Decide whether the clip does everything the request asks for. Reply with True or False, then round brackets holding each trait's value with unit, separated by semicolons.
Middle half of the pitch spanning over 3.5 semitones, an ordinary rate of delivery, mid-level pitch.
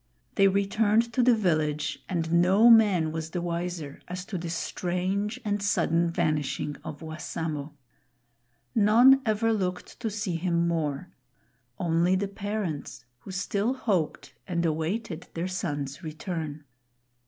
False (4.1 semitones; 130 wpm; 180 Hz)